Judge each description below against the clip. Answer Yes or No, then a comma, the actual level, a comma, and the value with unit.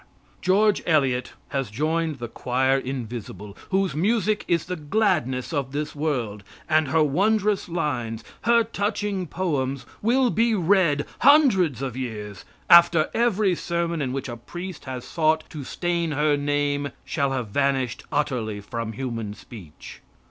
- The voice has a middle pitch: Yes, medium, 150 Hz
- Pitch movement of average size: No, wide, 6.1 semitones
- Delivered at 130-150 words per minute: Yes, average, 140 wpm